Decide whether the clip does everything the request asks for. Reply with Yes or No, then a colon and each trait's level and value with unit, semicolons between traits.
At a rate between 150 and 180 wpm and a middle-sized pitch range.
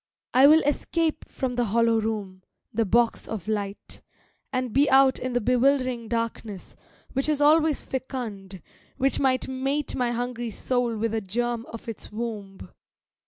Yes: average, 155 wpm; average, 3.1 semitones